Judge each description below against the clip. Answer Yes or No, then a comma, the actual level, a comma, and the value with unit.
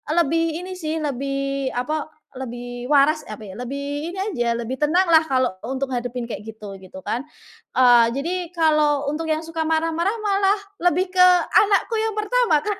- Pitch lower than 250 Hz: No, very high, 300 Hz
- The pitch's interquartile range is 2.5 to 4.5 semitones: No, wide, 5.4 semitones